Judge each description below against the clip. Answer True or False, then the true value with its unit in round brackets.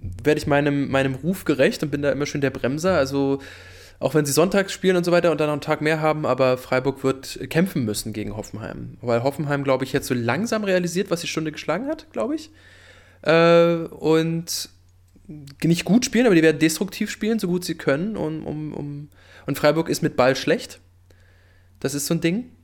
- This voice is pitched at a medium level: True (145 Hz)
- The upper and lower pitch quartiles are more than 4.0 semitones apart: True (4.7 semitones)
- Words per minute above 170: True (205 wpm)